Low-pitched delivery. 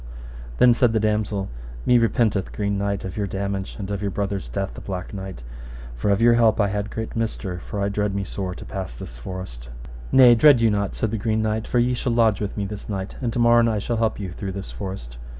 Yes: low, 100 Hz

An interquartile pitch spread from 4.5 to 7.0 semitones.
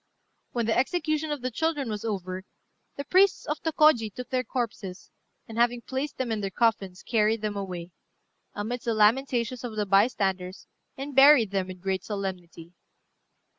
Yes: average, 5.1 semitones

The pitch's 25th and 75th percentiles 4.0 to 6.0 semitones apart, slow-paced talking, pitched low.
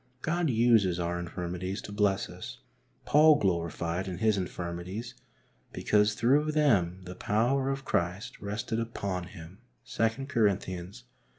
Yes: average, 4.7 semitones; slow, 130 wpm; low, 100 Hz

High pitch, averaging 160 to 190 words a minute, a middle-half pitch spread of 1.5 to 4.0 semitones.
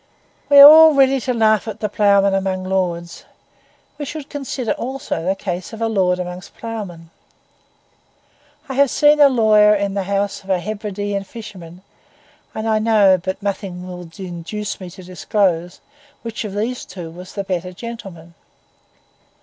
Yes: high, 200 Hz; average, 165 wpm; average, 3.6 semitones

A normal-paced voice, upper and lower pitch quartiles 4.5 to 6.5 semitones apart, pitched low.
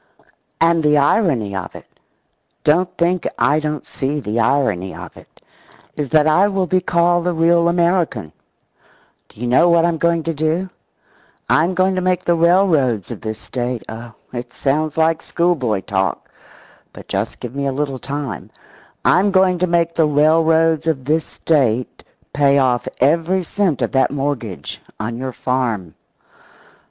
No: average, 160 wpm; average, 5.0 semitones; medium, 155 Hz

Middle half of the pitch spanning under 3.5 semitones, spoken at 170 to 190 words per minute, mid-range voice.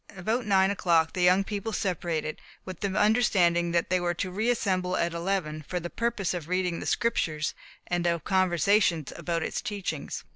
Yes: average, 2.7 semitones; average, 180 wpm; medium, 180 Hz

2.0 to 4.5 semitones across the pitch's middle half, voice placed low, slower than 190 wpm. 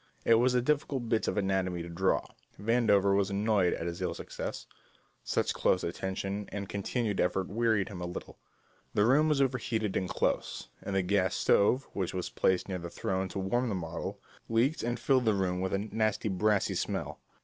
No: average, 3.4 semitones; low, 100 Hz; average, 195 wpm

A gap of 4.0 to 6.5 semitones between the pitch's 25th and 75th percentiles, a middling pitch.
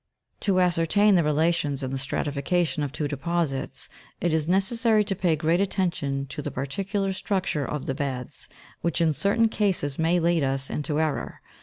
Yes: average, 4.6 semitones; medium, 165 Hz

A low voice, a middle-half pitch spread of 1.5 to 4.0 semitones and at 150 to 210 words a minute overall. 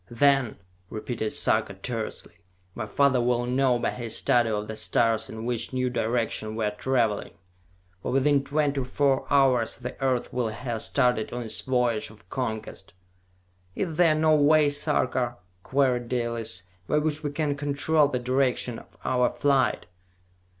Yes: low, 125 Hz; average, 3.4 semitones; average, 155 wpm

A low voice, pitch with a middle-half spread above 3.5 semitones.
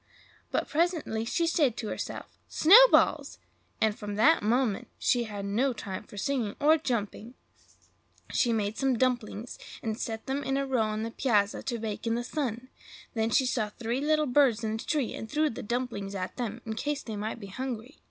No: high, 235 Hz; average, 3.9 semitones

